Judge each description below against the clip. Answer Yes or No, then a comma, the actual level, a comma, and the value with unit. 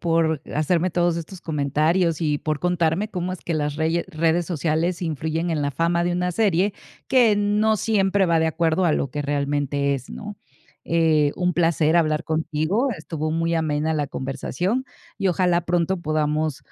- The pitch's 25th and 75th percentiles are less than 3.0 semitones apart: Yes, narrow, 2.5 semitones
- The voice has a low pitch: No, medium, 165 Hz